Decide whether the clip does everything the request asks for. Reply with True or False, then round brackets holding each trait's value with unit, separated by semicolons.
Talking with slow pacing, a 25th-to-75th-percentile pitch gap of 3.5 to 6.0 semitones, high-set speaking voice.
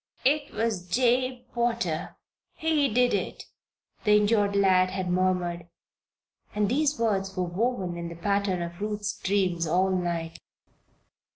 True (130 wpm; 4.6 semitones; 200 Hz)